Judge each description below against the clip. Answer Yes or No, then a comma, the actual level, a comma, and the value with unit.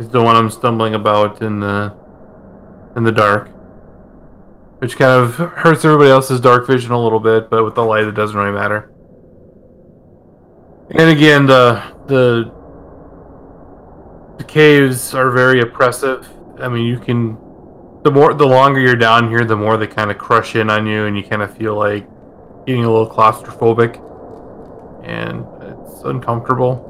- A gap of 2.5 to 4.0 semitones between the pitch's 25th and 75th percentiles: Yes, average, 3.1 semitones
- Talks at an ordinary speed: Yes, average, 160 wpm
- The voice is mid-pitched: No, low, 115 Hz